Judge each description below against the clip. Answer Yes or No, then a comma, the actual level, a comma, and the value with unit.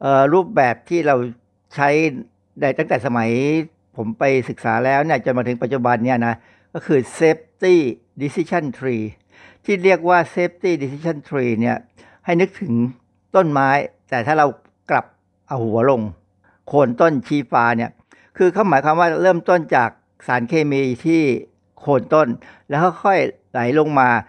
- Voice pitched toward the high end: No, medium, 140 Hz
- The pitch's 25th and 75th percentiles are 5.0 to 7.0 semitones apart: Yes, wide, 5.5 semitones